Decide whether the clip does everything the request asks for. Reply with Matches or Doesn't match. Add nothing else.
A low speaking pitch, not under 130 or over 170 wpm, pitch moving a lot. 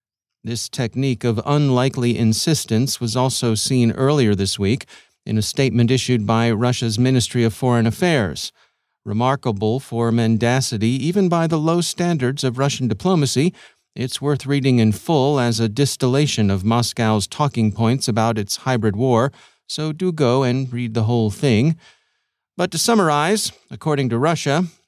Doesn't match